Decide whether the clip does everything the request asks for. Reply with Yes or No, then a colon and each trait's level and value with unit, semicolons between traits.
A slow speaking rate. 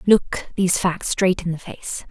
No: average, 200 wpm